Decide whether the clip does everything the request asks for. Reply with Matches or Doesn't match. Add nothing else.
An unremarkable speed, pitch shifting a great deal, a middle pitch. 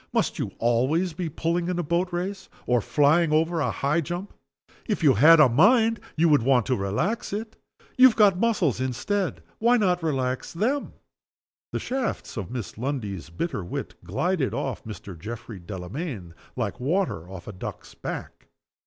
Matches